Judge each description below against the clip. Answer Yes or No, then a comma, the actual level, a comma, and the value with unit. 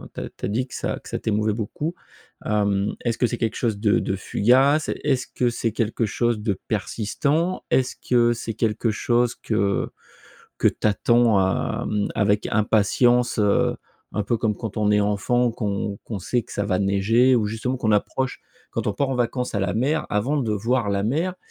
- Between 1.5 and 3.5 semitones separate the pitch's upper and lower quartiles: Yes, average, 3.1 semitones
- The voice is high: No, low, 115 Hz